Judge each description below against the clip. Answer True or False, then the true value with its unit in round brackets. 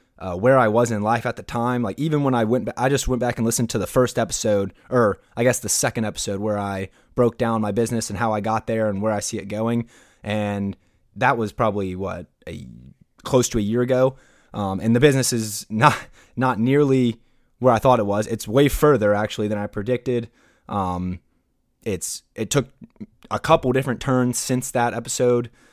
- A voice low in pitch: True (115 Hz)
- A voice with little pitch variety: False (3.2 semitones)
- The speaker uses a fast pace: True (210 wpm)